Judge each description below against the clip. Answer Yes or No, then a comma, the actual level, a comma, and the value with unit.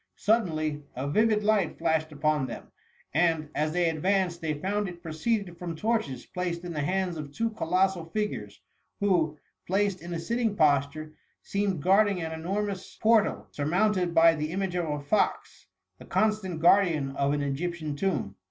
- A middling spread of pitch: Yes, average, 4.3 semitones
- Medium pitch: Yes, medium, 170 Hz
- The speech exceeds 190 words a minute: No, average, 160 wpm